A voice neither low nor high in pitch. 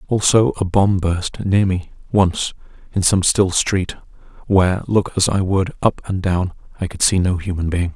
No: very low, 95 Hz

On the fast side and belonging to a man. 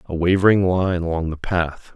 No: average, 185 wpm; male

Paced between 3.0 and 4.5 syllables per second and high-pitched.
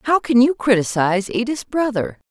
No: 5.1 syllables/s; high, 235 Hz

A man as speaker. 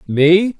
Yes: male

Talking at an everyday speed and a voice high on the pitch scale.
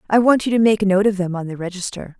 No: fast, 330 wpm; high, 200 Hz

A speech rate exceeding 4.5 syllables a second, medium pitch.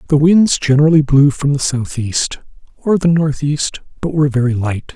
Yes: 4.9 syllables/s; medium, 145 Hz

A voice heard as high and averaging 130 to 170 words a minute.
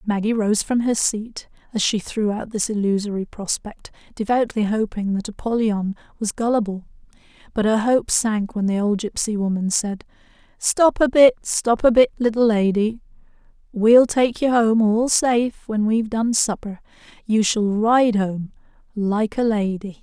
Yes: high, 220 Hz; average, 160 wpm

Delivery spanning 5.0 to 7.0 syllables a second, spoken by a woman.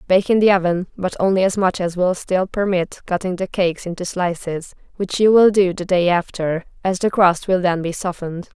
Yes: 5.3 syllables/s; female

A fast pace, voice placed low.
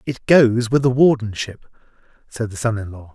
No: average, 190 wpm; low, 115 Hz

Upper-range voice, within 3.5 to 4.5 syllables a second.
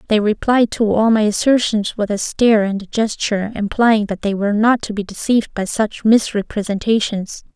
No: high, 215 Hz; 5.3 syllables/s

